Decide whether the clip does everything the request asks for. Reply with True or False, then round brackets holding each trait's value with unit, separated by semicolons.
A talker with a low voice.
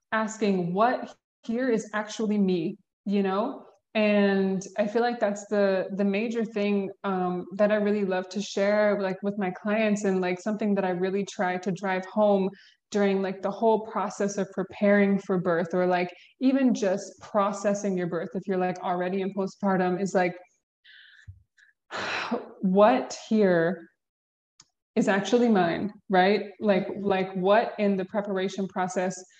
False (195 Hz)